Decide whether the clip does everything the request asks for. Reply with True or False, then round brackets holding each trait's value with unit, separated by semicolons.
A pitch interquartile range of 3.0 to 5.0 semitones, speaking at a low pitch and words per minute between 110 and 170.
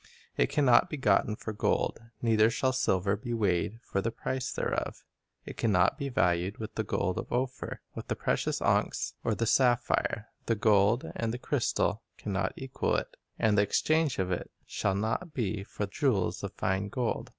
False (3.7 semitones; 110 Hz; 190 wpm)